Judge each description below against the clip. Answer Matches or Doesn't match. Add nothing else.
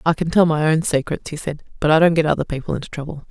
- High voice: Doesn't match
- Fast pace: Matches